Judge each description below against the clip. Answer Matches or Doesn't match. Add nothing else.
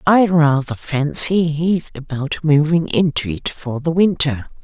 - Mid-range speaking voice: Matches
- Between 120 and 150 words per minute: Matches